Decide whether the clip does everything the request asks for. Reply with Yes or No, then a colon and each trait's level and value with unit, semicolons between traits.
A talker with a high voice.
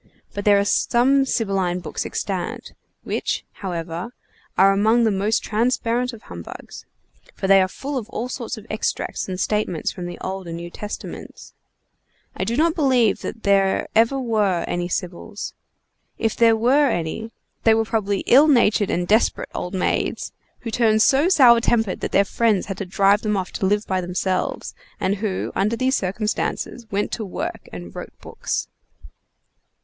Yes: high, 210 Hz